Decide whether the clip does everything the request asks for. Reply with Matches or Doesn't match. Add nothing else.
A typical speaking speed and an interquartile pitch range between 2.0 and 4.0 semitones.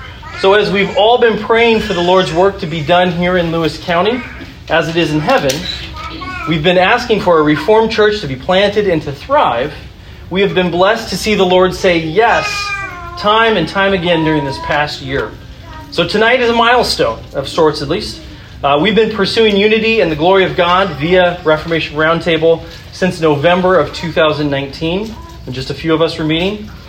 Doesn't match